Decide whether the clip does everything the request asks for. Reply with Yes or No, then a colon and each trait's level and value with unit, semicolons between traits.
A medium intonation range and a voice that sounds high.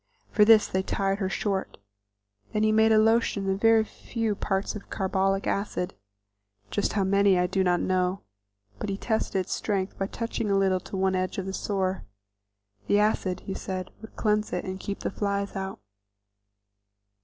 No: narrow, 1.8 semitones; high, 195 Hz